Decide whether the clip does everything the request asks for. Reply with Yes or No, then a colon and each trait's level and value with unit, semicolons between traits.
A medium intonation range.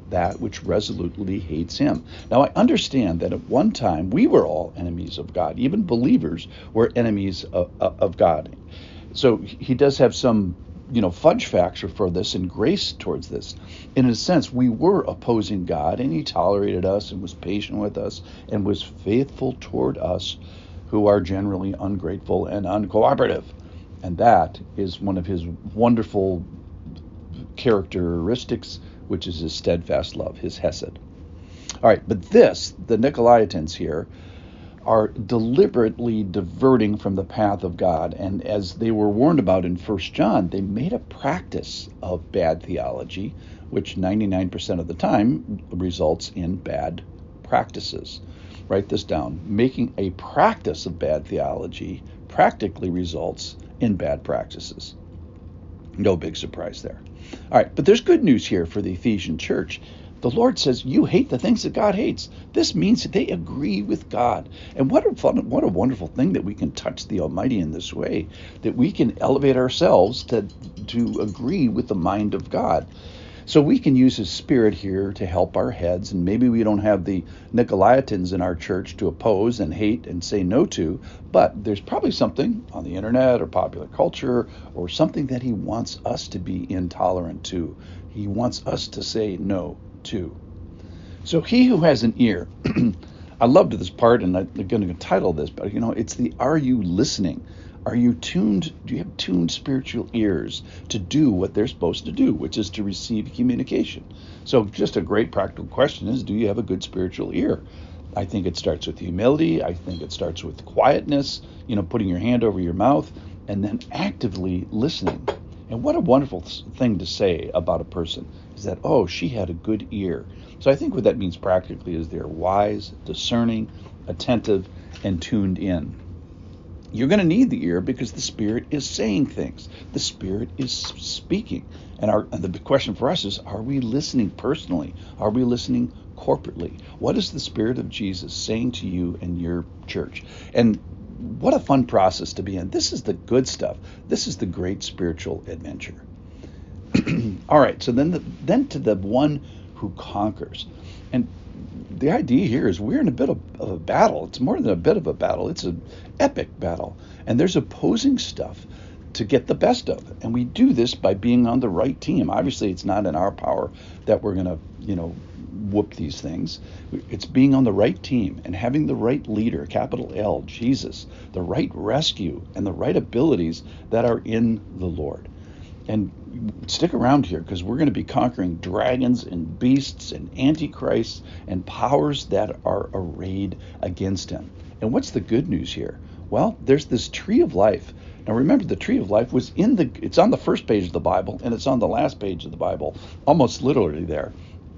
Yes: average, 4.7 semitones